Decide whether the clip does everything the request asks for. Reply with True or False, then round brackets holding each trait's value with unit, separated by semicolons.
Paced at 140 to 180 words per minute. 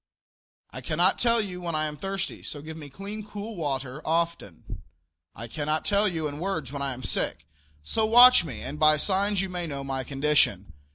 False (195 wpm)